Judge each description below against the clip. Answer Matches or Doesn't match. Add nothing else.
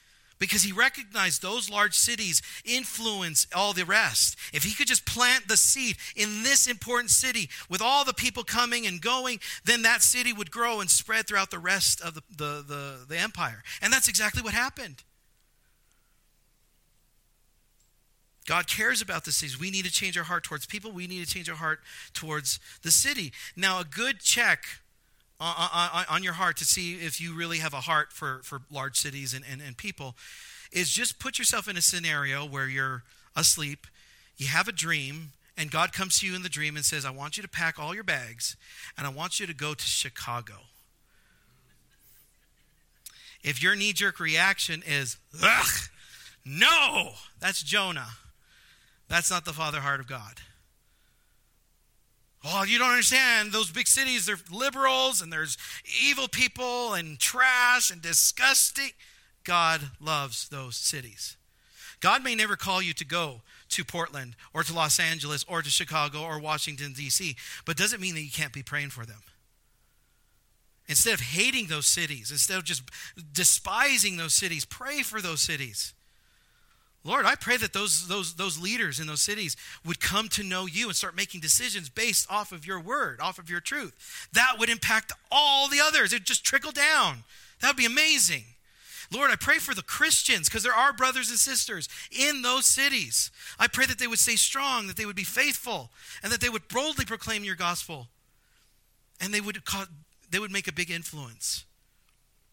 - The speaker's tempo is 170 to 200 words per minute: Matches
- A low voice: Doesn't match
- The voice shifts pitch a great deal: Matches